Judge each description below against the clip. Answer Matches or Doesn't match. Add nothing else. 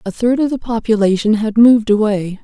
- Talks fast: Doesn't match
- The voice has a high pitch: Matches